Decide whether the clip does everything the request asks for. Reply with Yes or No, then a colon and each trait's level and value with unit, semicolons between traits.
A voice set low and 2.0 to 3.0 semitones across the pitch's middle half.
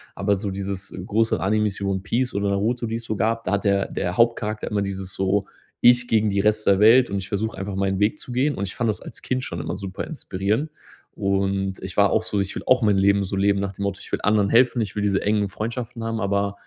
Yes: low, 100 Hz; narrow, 2.4 semitones